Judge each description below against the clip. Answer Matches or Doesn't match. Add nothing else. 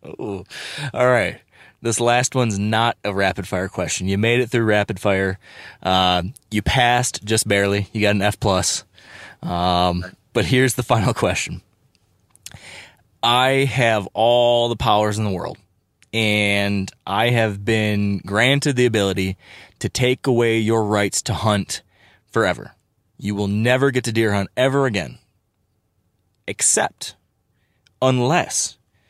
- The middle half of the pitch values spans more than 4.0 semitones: Doesn't match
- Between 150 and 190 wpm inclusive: Doesn't match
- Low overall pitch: Matches